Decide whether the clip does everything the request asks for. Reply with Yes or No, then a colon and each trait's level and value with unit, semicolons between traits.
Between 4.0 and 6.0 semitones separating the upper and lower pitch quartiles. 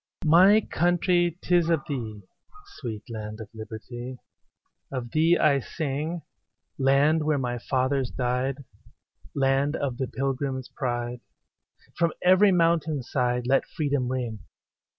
Yes: average, 4.3 semitones